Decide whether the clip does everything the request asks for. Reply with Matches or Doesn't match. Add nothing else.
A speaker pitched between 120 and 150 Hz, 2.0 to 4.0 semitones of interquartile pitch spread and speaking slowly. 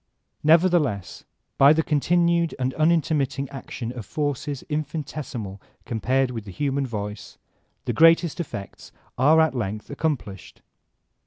Doesn't match